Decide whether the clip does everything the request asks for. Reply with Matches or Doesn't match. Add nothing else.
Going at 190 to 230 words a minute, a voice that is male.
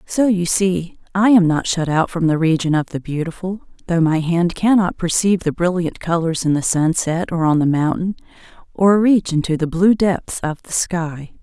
Doesn't match